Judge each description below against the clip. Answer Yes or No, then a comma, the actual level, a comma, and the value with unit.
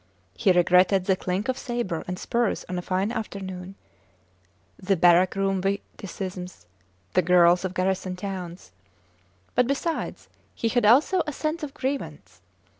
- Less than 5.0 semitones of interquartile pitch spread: Yes, average, 4.3 semitones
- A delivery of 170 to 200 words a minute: No, average, 140 wpm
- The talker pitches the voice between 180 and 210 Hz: Yes, high, 190 Hz